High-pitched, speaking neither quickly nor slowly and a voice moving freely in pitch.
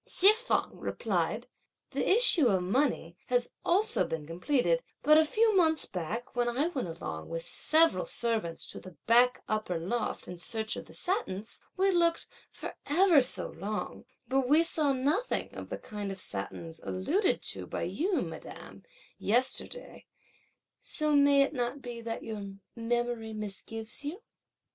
Yes: high, 245 Hz; average, 160 wpm; wide, 7.3 semitones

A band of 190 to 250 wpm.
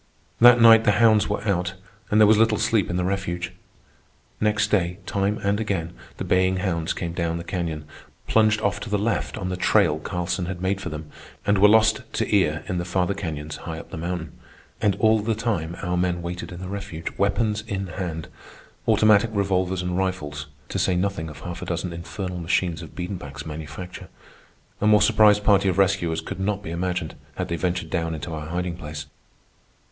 Yes: average, 195 wpm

